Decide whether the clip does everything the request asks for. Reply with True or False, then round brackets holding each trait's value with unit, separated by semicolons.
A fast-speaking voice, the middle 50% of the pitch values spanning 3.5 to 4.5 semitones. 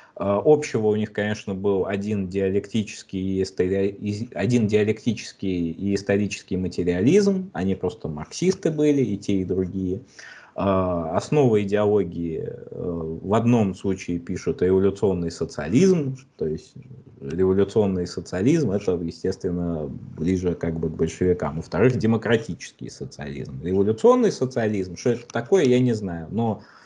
False (115 wpm; 3.8 semitones)